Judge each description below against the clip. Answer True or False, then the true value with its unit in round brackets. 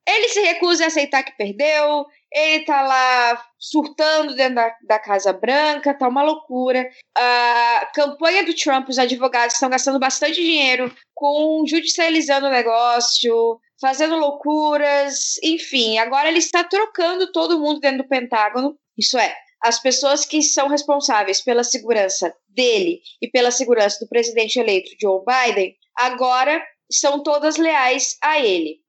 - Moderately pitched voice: False (275 Hz)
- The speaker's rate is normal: True (145 wpm)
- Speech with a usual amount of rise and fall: True (4.2 semitones)